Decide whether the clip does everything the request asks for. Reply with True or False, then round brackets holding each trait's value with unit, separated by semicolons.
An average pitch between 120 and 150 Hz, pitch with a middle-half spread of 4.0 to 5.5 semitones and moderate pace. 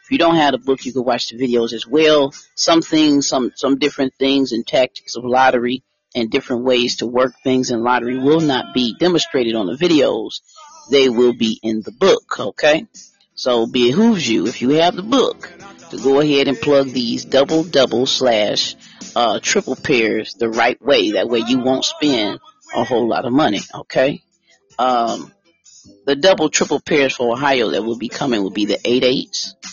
True (135 Hz; 4.7 semitones; 190 wpm)